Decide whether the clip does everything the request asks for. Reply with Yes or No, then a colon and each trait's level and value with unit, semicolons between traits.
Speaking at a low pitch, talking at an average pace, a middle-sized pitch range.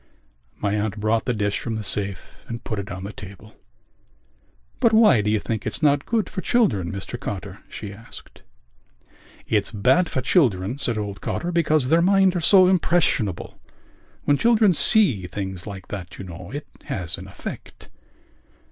No: low, 110 Hz; average, 170 wpm; wide, 8.7 semitones